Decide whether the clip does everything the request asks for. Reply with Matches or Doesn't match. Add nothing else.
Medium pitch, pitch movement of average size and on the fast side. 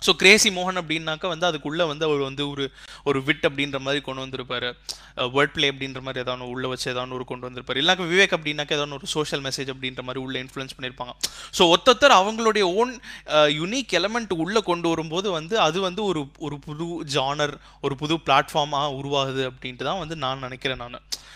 Matches